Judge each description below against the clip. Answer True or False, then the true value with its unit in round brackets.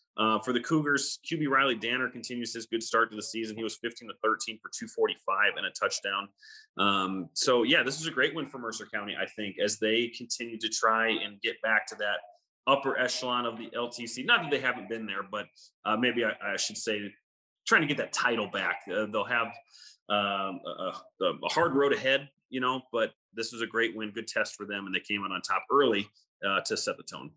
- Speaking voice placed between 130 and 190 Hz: False (115 Hz)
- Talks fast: True (230 wpm)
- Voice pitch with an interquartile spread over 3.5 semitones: False (2.9 semitones)